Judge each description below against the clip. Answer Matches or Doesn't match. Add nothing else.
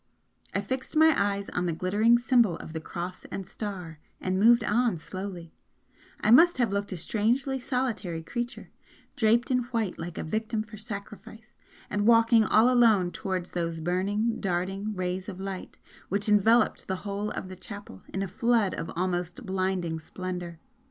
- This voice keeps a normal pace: Matches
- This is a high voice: Matches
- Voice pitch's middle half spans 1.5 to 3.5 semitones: Doesn't match